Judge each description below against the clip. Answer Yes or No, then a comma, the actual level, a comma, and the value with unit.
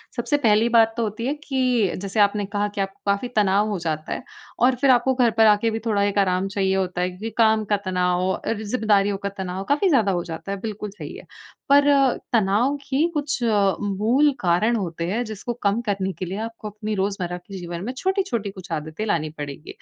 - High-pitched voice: Yes, high, 205 Hz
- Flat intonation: No, average, 3.3 semitones